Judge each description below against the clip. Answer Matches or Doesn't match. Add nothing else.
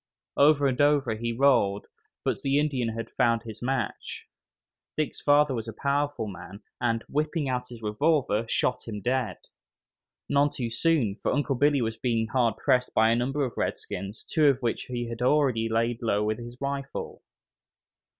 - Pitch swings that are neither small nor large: Matches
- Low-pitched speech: Matches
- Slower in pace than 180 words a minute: Matches